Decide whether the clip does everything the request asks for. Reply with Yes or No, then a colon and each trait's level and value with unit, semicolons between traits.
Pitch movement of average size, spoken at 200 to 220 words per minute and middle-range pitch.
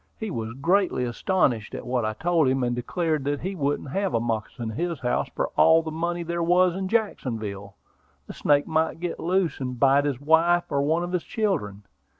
No: wide, 6.1 semitones; fast, 205 wpm; medium, 155 Hz